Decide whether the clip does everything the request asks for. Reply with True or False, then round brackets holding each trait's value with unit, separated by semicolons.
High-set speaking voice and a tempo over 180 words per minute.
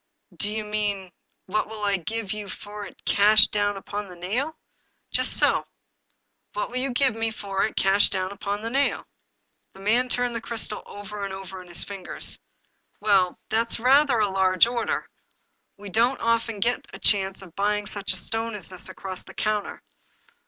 True (210 Hz; 195 wpm)